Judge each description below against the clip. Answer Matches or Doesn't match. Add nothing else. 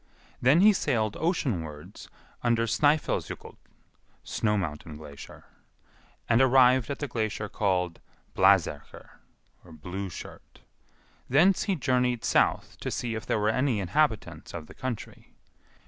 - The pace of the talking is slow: Matches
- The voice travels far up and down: Matches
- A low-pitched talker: Matches